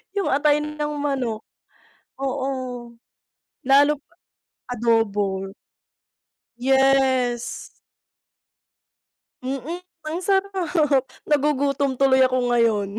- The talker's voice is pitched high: Yes, very high, 270 Hz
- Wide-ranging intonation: No, average, 3.3 semitones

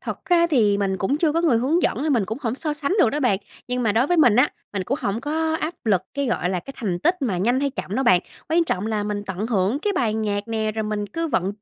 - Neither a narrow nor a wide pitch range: No, wide, 6.4 semitones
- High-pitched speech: Yes, high, 235 Hz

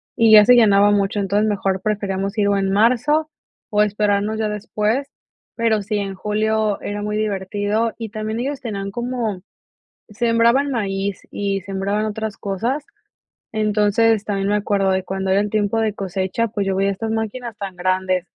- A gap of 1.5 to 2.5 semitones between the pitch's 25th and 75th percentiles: Yes, narrow, 2.0 semitones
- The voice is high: Yes, high, 210 Hz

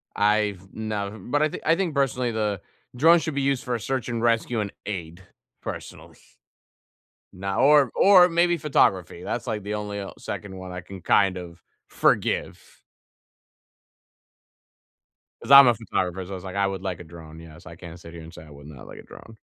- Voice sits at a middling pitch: No, low, 105 Hz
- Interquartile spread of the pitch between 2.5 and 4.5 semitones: No, wide, 5.5 semitones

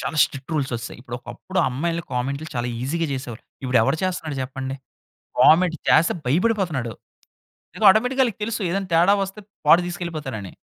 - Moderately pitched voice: Yes, medium, 155 Hz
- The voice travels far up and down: Yes, wide, 6.0 semitones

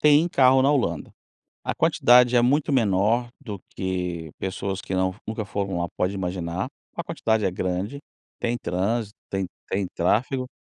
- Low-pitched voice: Yes, low, 100 Hz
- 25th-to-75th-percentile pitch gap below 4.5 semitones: No, average, 4.8 semitones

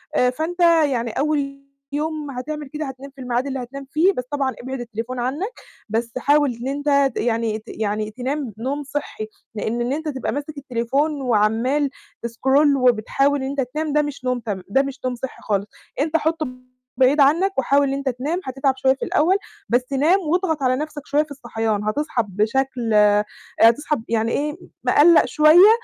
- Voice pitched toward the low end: No, very high, 270 Hz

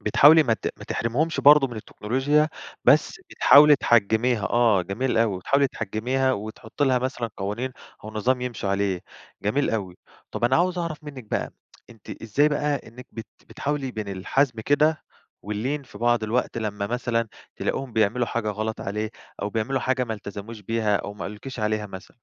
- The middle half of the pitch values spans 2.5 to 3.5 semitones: No, average, 3.9 semitones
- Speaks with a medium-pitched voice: No, low, 115 Hz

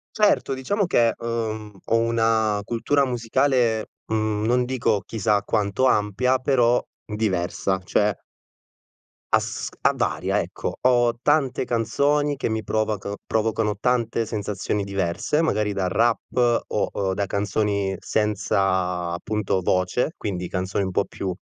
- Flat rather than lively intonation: No, average, 3.3 semitones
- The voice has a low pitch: Yes, low, 110 Hz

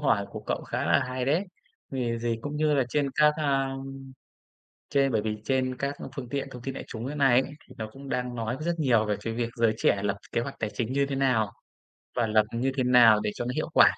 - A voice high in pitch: No, low, 125 Hz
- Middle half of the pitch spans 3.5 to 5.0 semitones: No, average, 3.1 semitones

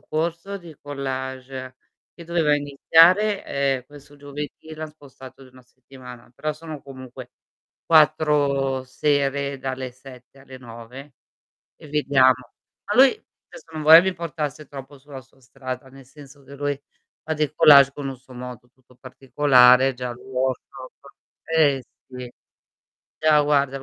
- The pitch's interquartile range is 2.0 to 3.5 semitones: Yes, narrow, 2.5 semitones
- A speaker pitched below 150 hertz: Yes, medium, 140 Hz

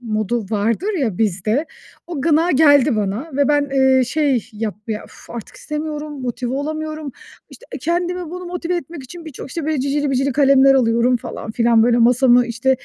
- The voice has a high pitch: Yes, very high, 270 Hz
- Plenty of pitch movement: No, average, 4.6 semitones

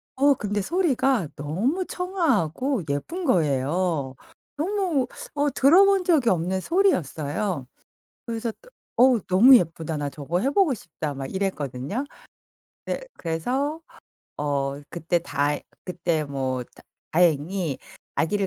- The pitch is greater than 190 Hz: No, medium, 185 Hz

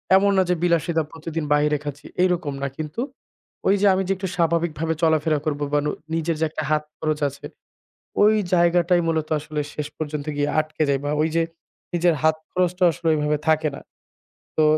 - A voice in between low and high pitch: Yes, medium, 160 Hz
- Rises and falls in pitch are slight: Yes, narrow, 2.3 semitones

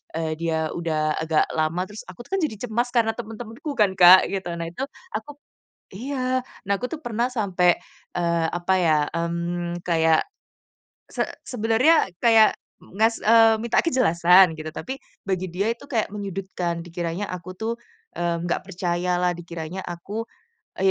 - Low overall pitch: No, medium, 185 Hz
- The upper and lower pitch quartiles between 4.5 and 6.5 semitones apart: Yes, average, 4.8 semitones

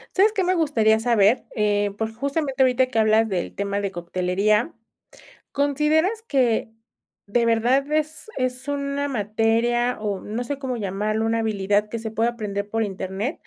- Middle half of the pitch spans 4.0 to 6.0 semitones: Yes, average, 4.5 semitones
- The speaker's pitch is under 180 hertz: No, high, 230 Hz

